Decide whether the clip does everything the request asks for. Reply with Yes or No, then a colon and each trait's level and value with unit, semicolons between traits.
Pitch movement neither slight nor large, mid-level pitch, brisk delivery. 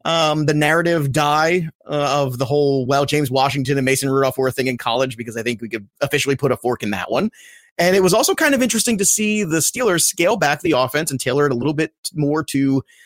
Yes: average, 3.5 semitones; medium, 145 Hz; fast, 250 wpm